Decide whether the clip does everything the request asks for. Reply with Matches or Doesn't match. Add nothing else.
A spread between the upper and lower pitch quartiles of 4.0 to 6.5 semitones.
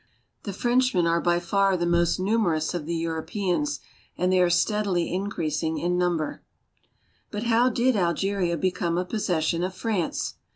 Doesn't match